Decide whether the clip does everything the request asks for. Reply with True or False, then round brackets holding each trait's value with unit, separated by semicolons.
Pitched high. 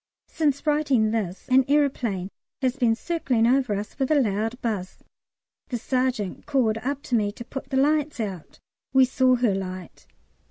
True (245 Hz)